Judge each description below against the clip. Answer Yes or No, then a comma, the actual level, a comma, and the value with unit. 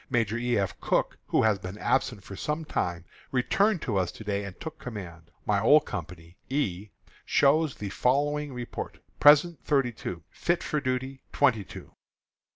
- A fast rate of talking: No, average, 165 wpm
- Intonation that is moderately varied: No, wide, 6.7 semitones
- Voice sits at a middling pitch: No, low, 120 Hz